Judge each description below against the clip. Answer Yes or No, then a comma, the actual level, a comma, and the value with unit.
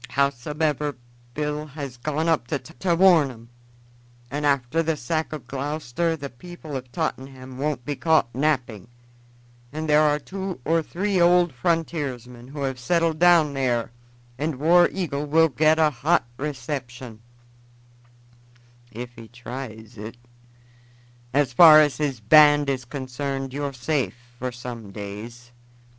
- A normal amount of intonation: Yes, average, 4.1 semitones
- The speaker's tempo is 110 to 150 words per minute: Yes, average, 140 wpm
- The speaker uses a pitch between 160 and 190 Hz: No, medium, 140 Hz